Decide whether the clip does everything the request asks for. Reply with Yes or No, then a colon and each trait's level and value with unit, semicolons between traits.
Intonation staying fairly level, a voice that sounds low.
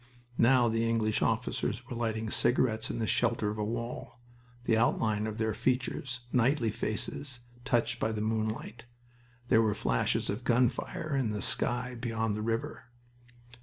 Yes: narrow, 1.9 semitones; low, 115 Hz